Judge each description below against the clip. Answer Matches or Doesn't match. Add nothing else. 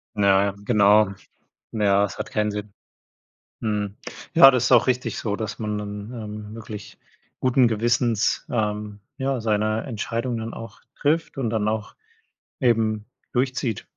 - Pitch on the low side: Matches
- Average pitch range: Doesn't match